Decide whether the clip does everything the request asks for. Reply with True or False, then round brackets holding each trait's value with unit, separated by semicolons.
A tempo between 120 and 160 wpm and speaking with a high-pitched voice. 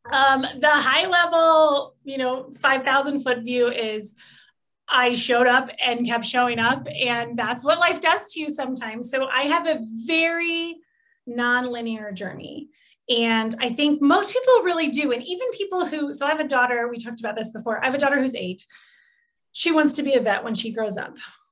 False (190 wpm; 265 Hz)